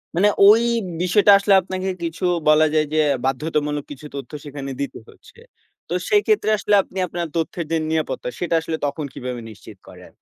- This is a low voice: No, medium, 160 Hz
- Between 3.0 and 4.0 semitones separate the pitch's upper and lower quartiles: No, average, 4.5 semitones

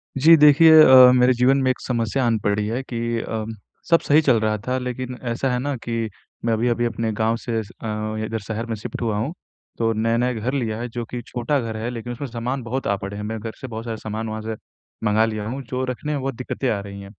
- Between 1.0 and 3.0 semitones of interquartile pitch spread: Yes, narrow, 2.5 semitones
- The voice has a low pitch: Yes, low, 115 Hz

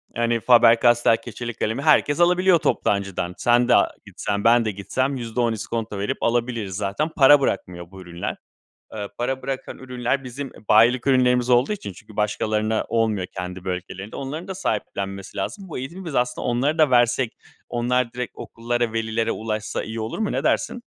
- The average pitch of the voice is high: No, low, 120 Hz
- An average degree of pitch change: Yes, average, 3.4 semitones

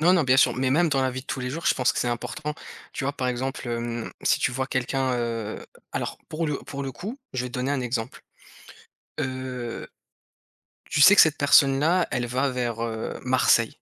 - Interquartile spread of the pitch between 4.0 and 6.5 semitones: No, narrow, 2.5 semitones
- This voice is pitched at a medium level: No, low, 130 Hz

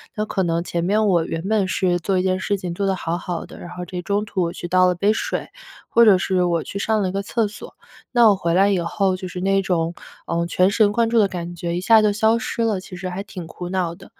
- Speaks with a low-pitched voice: No, medium, 185 Hz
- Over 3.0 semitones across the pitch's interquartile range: No, average, 2.7 semitones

